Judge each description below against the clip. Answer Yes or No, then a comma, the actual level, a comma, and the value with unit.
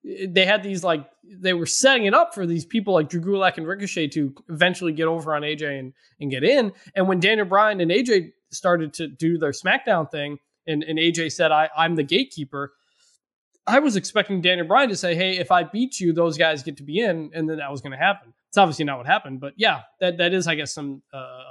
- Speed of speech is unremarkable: No, fast, 240 wpm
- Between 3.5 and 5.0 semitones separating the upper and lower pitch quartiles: Yes, average, 4.1 semitones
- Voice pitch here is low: No, medium, 170 Hz